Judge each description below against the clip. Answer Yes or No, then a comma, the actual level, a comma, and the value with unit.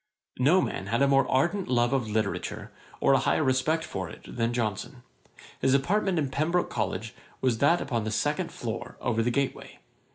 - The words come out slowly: No, average, 185 wpm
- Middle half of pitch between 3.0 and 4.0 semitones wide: No, average, 4.7 semitones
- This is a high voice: No, low, 130 Hz